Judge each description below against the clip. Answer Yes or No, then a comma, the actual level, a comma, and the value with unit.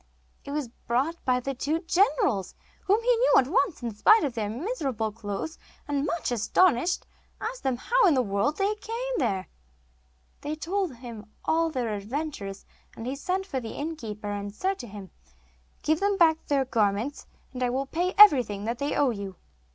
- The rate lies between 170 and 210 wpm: Yes, average, 180 wpm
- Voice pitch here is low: No, very high, 275 Hz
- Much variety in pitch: Yes, wide, 7.1 semitones